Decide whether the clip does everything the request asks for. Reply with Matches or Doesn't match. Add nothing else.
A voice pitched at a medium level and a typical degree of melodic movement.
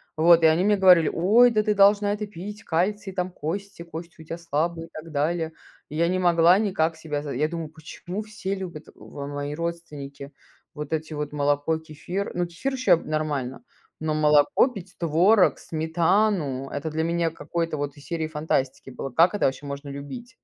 Matches